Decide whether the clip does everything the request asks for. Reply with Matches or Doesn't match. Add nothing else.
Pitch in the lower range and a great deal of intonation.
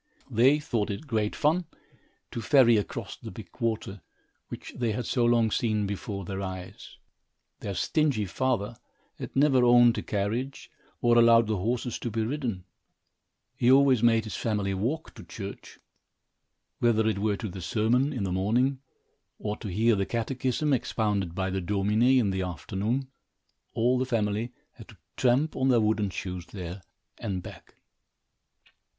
Doesn't match